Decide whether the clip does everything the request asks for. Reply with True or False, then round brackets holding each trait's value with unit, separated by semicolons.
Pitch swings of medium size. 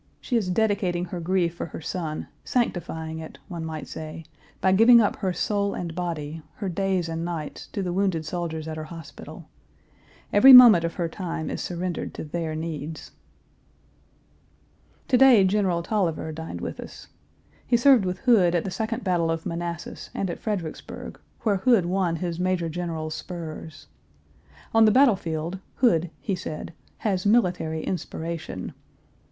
True (3.4 semitones)